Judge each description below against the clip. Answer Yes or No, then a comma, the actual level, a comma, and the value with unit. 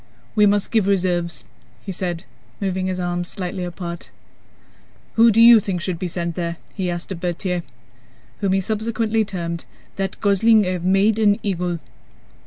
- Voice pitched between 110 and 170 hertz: No, medium, 185 Hz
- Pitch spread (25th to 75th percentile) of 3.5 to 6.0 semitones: No, average, 2.7 semitones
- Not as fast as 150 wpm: No, average, 165 wpm